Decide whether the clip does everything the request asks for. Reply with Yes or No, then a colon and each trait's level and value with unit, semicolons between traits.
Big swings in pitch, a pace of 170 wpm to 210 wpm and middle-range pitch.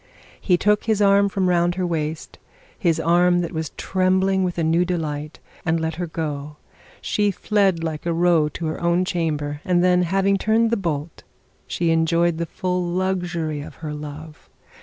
No: narrow, 2.5 semitones; average, 180 wpm; medium, 175 Hz